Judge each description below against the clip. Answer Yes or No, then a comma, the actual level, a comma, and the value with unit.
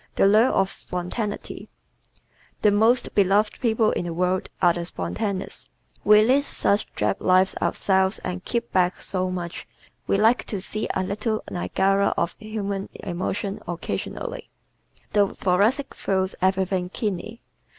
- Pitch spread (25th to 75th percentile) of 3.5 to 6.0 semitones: No, average, 2.7 semitones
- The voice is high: Yes, high, 195 Hz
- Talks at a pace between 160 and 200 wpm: No, average, 140 wpm